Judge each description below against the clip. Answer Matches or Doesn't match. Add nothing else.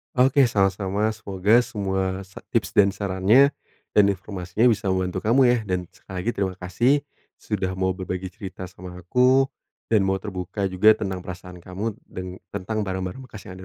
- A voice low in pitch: Matches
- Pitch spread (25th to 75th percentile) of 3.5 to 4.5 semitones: Doesn't match